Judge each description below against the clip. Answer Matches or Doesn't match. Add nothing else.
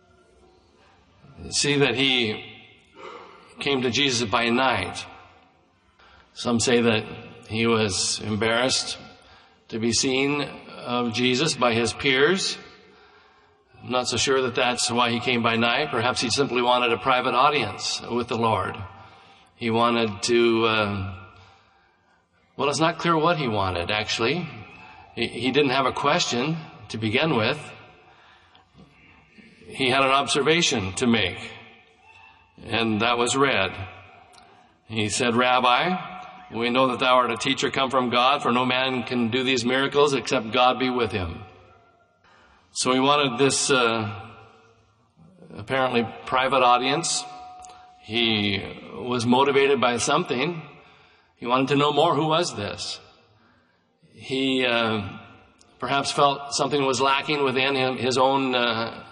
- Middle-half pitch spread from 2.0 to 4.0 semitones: Matches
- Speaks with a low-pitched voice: Matches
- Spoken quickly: Doesn't match